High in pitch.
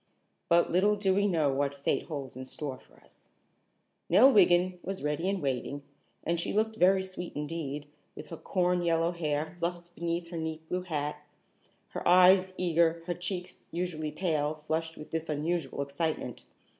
No: medium, 170 Hz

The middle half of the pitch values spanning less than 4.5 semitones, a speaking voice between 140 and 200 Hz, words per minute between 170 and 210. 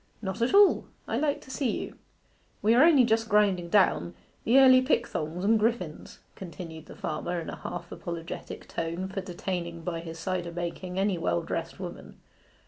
No: average, 4.9 semitones; medium, 185 Hz; average, 175 wpm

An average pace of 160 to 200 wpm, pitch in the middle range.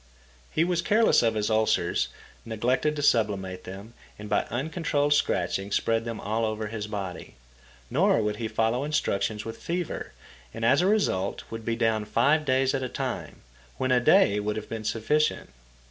No: average, 175 wpm; low, 115 Hz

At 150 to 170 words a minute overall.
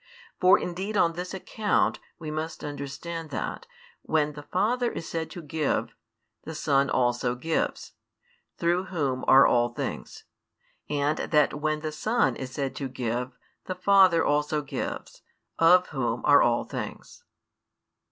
No: average, 140 wpm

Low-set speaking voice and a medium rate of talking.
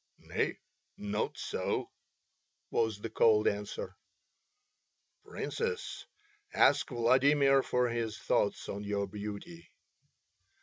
No: low, 110 Hz; slow, 90 wpm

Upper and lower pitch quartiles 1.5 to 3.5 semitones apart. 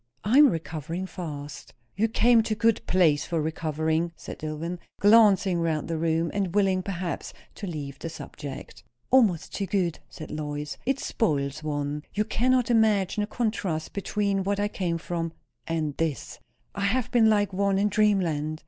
No: average, 4.8 semitones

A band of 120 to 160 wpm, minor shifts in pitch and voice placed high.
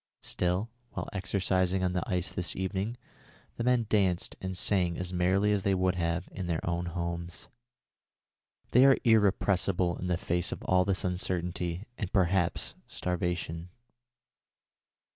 No: average, 145 wpm; narrow, 1.8 semitones; very low, 90 Hz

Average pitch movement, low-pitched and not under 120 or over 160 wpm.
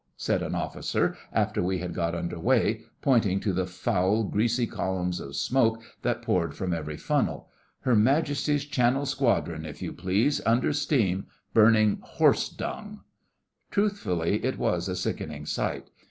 No: wide, 6.0 semitones; low, 105 Hz; average, 150 wpm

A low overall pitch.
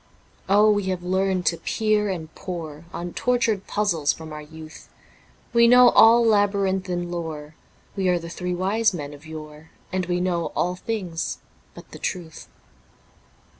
No: medium, 180 Hz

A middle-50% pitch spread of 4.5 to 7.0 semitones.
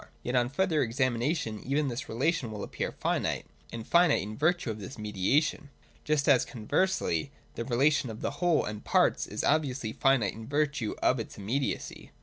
Yes: average, 5.2 semitones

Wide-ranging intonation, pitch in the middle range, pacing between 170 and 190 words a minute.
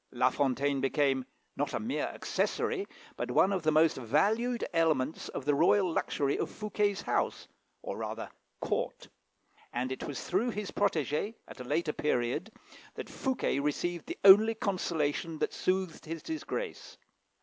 No: wide, 6.4 semitones; medium, 165 Hz; average, 150 wpm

